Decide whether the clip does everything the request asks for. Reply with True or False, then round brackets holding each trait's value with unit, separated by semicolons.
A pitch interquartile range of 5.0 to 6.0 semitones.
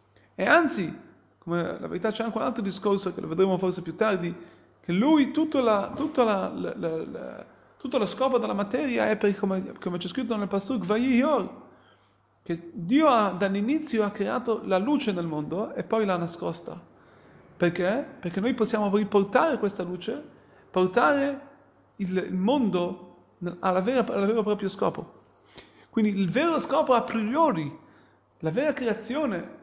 True (5.4 semitones)